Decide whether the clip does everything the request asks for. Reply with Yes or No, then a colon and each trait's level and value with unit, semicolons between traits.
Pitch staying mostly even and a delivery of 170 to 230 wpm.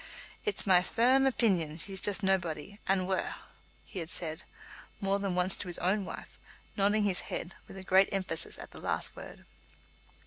Yes: narrow, 2.0 semitones; average, 175 wpm